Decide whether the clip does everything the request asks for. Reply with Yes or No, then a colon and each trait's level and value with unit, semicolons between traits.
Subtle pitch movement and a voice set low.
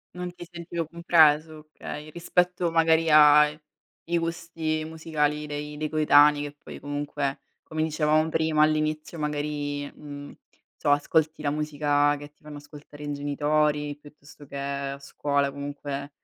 No: narrow, 1.5 semitones; medium, 150 Hz